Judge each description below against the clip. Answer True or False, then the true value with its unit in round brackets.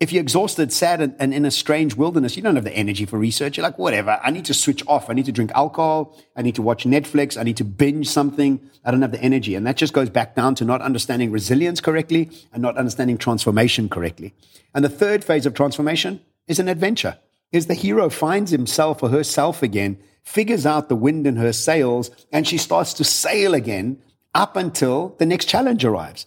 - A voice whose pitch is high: False (140 Hz)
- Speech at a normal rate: False (220 wpm)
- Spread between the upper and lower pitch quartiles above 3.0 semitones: True (4.6 semitones)